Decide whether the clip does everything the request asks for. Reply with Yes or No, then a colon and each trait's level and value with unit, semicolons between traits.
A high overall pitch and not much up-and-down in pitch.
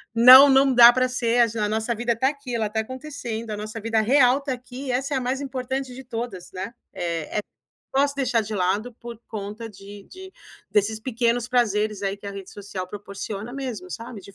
No: high, 235 Hz; average, 3.5 semitones